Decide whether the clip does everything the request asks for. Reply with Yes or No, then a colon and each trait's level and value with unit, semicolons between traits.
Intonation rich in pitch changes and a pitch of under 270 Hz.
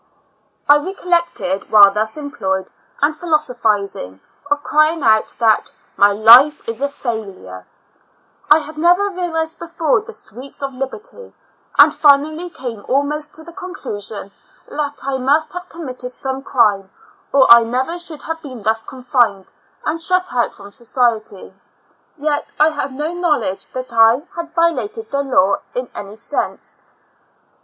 No: wide, 6.1 semitones; very high, 275 Hz